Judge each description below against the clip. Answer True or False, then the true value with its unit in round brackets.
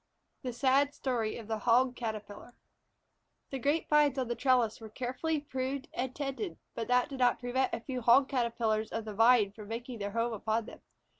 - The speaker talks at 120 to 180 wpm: False (195 wpm)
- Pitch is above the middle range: True (245 Hz)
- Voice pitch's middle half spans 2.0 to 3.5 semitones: True (2.8 semitones)